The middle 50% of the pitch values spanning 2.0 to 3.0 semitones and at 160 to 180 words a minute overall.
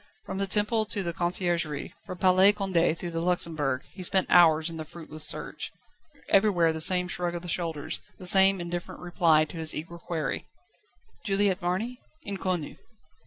Yes: average, 2.7 semitones; average, 165 wpm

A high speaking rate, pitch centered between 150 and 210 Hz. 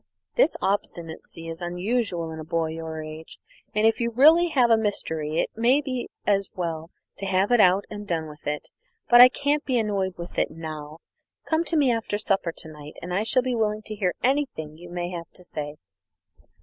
Yes: fast, 215 wpm; high, 190 Hz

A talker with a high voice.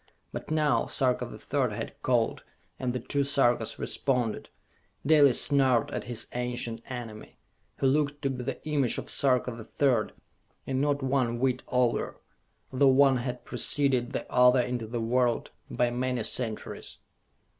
No: low, 125 Hz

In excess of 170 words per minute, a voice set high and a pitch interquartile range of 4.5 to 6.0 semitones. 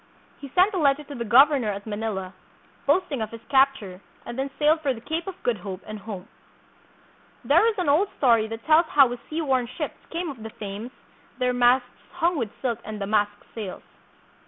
Yes: average, 200 wpm; very high, 250 Hz; wide, 5.5 semitones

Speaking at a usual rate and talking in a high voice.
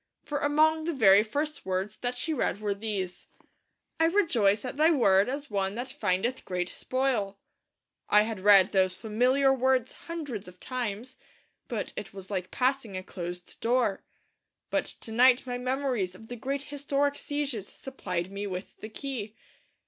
Yes: average, 165 wpm; high, 235 Hz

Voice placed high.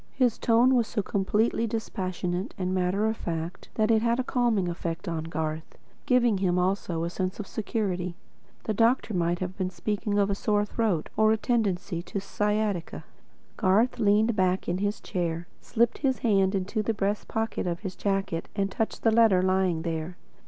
Yes: high, 200 Hz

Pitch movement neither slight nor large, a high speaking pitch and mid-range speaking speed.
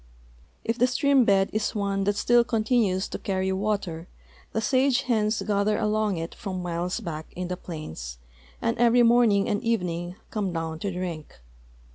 Yes: average, 4.1 semitones; high, 200 Hz; average, 170 wpm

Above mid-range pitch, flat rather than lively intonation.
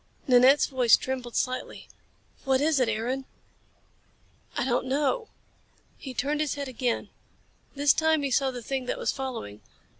Yes: very high, 265 Hz; narrow, 2.2 semitones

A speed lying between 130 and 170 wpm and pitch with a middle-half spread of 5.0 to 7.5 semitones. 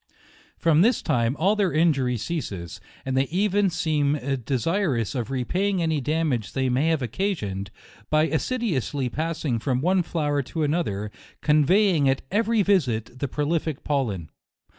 Yes: average, 145 wpm; wide, 5.4 semitones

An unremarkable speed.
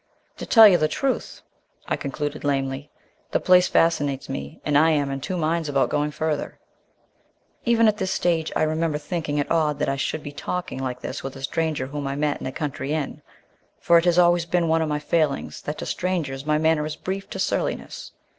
No: fast, 215 wpm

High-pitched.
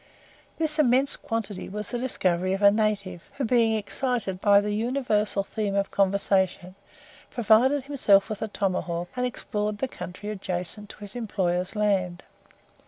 Yes: high, 210 Hz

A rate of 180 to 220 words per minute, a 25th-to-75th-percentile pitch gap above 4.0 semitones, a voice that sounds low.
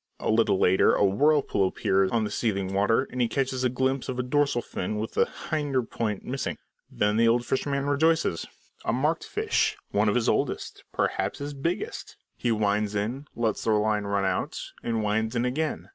Yes: average, 190 wpm; average, 4.6 semitones; low, 115 Hz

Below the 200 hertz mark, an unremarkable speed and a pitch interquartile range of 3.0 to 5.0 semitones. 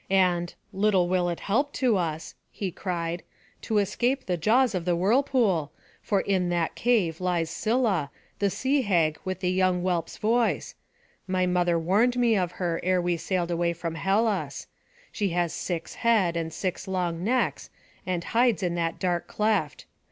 Yes: medium, 185 Hz; average, 165 wpm; average, 3.6 semitones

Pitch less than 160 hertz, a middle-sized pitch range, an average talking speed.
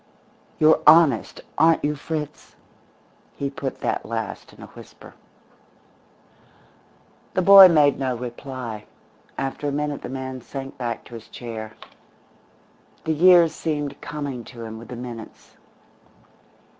No: low, 135 Hz; average, 4.1 semitones; slow, 130 wpm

